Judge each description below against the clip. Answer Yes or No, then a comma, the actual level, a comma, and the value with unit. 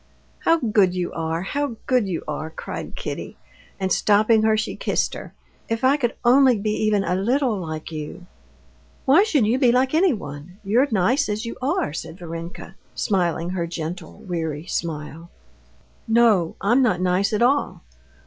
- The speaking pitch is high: Yes, high, 205 Hz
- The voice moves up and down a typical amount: No, wide, 6.0 semitones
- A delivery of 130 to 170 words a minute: Yes, average, 165 wpm